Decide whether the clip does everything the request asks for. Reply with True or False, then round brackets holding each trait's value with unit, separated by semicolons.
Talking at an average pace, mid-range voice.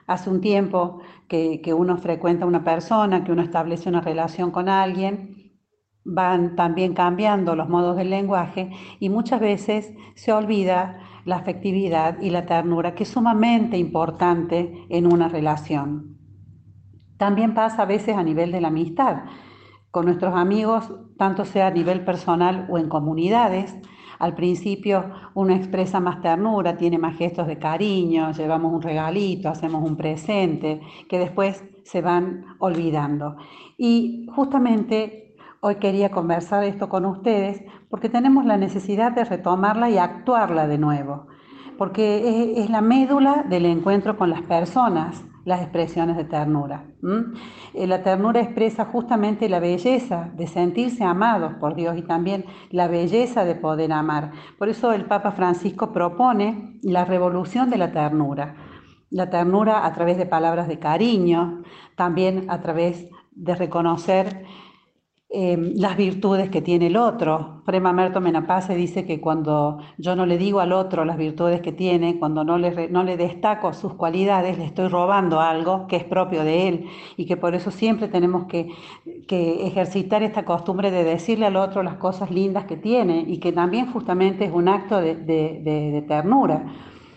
True (155 wpm; 180 Hz)